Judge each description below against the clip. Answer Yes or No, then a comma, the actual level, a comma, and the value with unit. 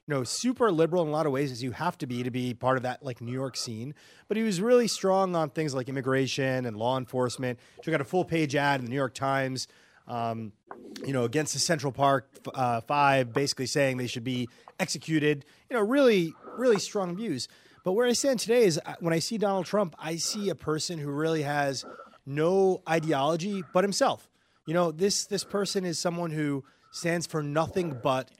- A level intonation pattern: No, wide, 5.4 semitones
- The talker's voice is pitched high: No, medium, 155 Hz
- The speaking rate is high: Yes, fast, 210 wpm